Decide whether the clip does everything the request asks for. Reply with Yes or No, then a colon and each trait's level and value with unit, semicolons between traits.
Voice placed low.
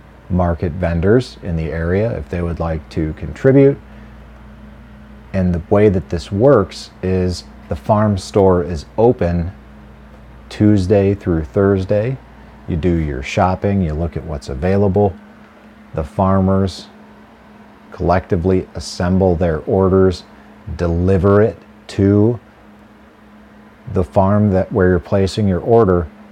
Yes: very low, 95 Hz